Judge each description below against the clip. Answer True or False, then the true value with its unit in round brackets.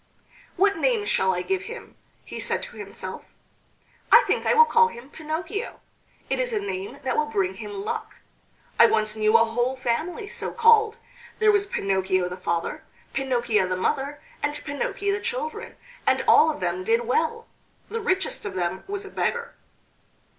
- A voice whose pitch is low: False (340 Hz)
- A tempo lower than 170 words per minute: False (175 wpm)